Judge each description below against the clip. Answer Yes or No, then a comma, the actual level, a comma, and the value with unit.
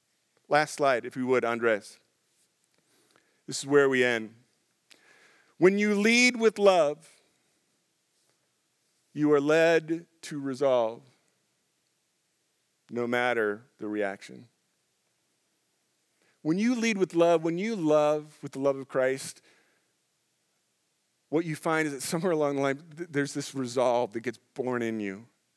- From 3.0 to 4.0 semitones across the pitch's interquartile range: No, average, 5.0 semitones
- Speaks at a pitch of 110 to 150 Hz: Yes, medium, 140 Hz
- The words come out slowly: Yes, slow, 130 wpm